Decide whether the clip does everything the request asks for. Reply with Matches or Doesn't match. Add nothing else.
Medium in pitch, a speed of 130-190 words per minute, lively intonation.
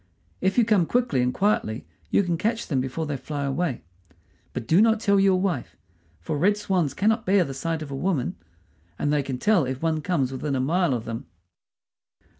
Doesn't match